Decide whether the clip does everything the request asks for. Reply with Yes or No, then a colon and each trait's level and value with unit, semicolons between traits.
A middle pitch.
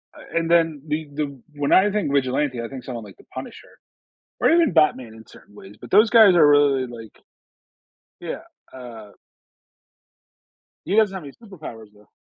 Yes: medium, 145 Hz